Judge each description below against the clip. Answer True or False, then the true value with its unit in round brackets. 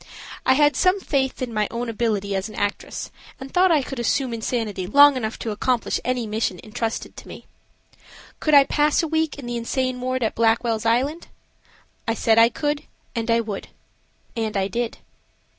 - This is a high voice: True (235 Hz)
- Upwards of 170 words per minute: True (185 wpm)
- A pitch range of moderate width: True (3.5 semitones)